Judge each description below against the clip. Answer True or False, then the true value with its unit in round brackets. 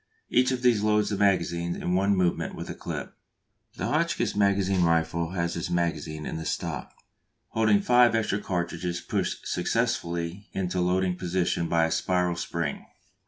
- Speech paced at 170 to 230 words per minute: False (160 wpm)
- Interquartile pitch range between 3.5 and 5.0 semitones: False (2.9 semitones)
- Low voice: True (90 Hz)